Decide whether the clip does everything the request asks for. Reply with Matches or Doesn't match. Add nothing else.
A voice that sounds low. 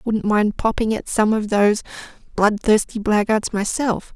Doesn't match